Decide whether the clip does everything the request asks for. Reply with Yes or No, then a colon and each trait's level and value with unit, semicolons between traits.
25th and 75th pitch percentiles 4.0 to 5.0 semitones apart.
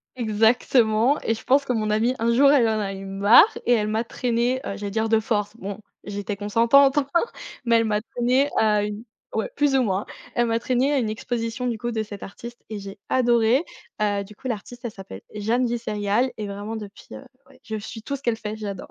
No: average, 2.7 semitones